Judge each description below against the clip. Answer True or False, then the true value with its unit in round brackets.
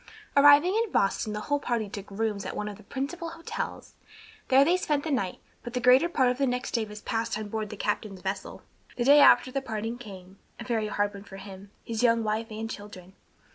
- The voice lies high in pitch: True (225 Hz)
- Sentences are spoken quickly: True (225 wpm)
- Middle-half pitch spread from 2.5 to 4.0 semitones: False (4.5 semitones)